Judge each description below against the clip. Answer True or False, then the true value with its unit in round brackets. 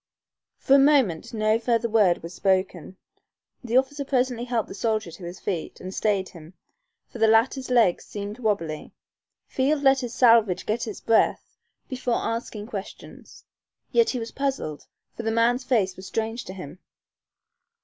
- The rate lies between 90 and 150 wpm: False (160 wpm)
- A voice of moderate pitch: False (225 Hz)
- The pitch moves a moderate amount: True (4.6 semitones)